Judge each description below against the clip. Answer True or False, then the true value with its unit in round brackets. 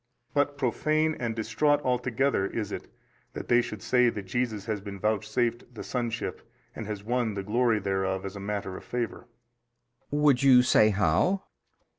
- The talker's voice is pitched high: False (115 Hz)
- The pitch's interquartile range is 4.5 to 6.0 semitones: False (3.5 semitones)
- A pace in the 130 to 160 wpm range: False (170 wpm)